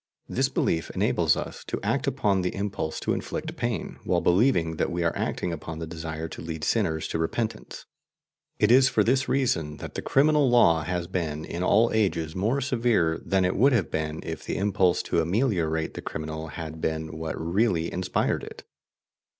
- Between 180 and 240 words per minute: Yes, average, 185 wpm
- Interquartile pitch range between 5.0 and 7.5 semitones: Yes, average, 5.3 semitones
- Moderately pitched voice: No, very low, 85 Hz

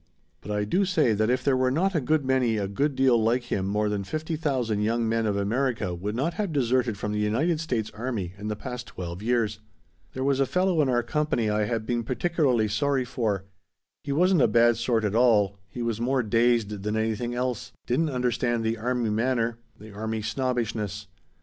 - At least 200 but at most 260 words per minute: Yes, fast, 205 wpm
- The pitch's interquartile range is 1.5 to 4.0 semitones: Yes, average, 3.5 semitones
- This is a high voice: No, low, 120 Hz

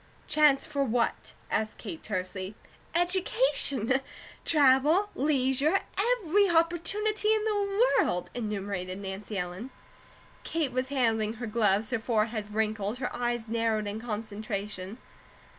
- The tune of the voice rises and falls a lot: Yes, wide, 7.1 semitones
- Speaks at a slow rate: Yes, slow, 115 wpm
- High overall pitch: Yes, high, 240 Hz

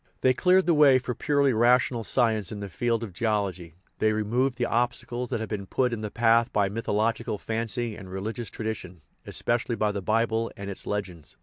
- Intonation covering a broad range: No, average, 2.8 semitones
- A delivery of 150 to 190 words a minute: No, average, 200 wpm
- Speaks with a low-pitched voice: Yes, low, 115 Hz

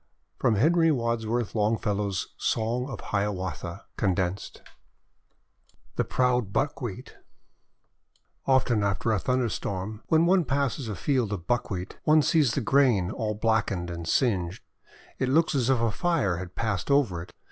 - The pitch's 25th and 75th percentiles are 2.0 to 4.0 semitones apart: No, average, 5.0 semitones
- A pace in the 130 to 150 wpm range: Yes, average, 145 wpm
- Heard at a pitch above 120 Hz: No, low, 110 Hz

